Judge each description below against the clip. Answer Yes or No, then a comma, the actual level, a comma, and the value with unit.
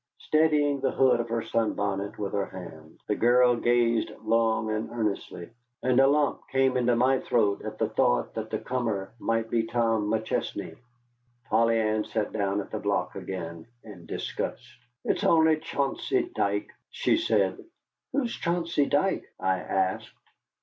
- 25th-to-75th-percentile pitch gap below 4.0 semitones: No, average, 4.4 semitones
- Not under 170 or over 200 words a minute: No, average, 155 wpm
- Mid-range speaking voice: No, low, 115 Hz